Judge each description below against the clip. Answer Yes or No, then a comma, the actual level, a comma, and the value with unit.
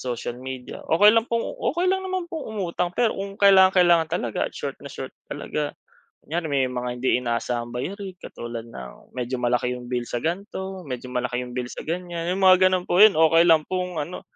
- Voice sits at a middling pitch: Yes, medium, 165 Hz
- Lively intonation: Yes, wide, 7.3 semitones